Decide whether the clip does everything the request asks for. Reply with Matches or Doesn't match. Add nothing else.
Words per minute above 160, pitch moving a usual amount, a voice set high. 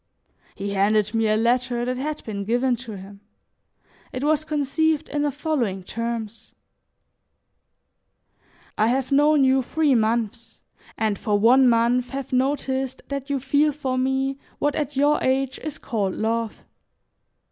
Doesn't match